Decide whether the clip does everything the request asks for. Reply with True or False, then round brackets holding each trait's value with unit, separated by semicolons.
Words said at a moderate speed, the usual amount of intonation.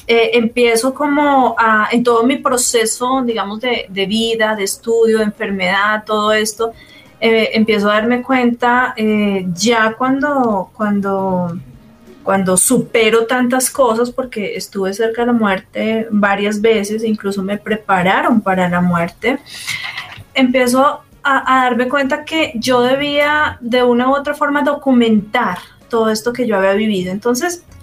True (140 wpm; 3.4 semitones)